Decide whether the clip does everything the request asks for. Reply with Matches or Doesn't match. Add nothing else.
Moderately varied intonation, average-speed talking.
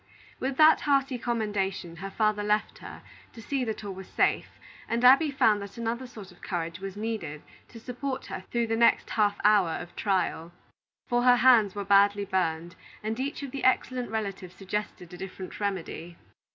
Matches